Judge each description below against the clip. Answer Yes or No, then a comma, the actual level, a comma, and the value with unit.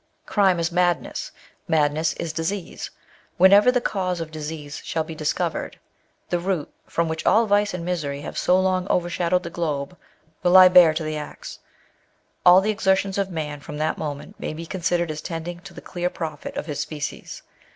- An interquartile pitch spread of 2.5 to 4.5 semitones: Yes, average, 2.9 semitones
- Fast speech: No, average, 185 wpm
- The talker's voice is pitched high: No, medium, 170 Hz